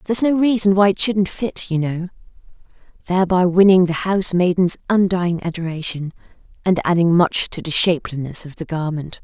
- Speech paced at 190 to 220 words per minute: No, average, 165 wpm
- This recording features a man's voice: No, female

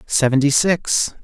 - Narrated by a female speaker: No, male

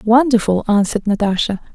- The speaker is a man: No, female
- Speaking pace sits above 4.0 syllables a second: Yes, 5.9 syllables/s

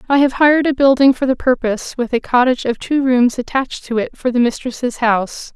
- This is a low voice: No, very high, 255 Hz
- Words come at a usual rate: No, fast, 225 wpm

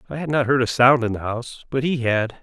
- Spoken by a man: Yes, male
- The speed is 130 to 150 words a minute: No, fast, 295 wpm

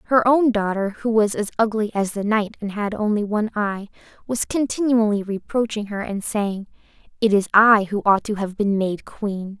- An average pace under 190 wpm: No, average, 195 wpm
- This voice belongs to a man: No, female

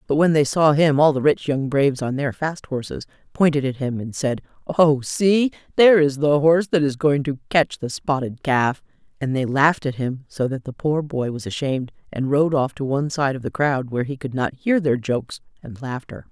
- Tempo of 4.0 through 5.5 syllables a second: Yes, 5.3 syllables/s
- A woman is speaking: Yes, female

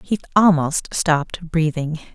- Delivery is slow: Yes, slow, 110 wpm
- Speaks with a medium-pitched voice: Yes, medium, 165 Hz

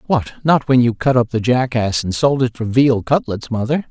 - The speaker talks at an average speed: No, fast, 230 wpm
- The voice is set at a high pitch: No, low, 125 Hz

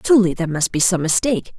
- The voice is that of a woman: Yes, female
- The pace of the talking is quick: Yes, fast, 230 wpm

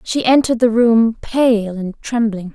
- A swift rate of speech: No, average, 140 wpm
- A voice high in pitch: Yes, high, 230 Hz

